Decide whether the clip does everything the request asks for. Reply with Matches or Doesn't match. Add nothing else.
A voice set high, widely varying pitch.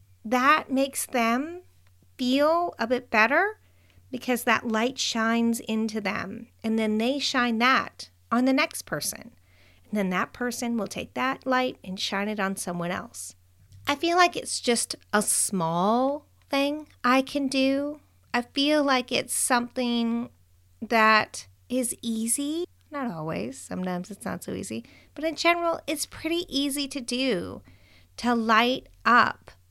Matches